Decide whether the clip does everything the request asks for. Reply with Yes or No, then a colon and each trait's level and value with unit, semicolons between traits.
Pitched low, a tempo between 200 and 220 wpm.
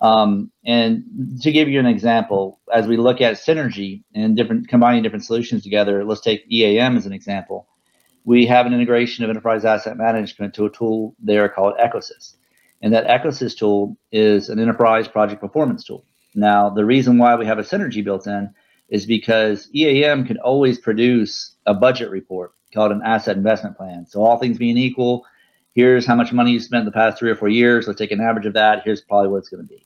Yes: low, 115 Hz; fast, 205 wpm